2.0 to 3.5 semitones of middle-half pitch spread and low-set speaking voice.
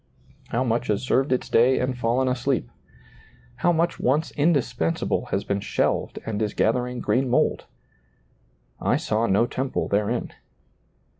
Yes: average, 2.9 semitones; low, 125 Hz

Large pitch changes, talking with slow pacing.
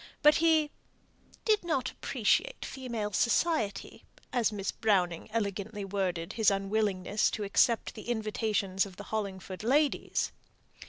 No: average, 3.7 semitones; slow, 120 wpm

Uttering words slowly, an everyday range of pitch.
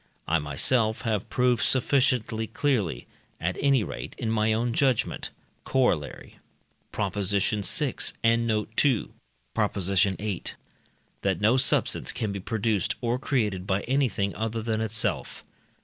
Yes: slow, 130 wpm; average, 3.6 semitones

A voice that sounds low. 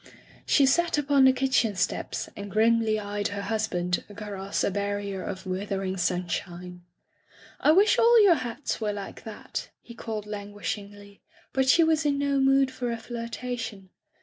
No: high, 215 Hz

